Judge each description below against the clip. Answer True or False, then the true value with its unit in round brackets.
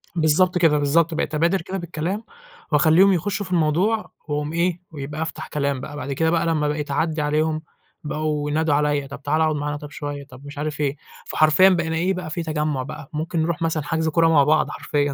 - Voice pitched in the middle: True (155 Hz)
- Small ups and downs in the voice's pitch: True (2.2 semitones)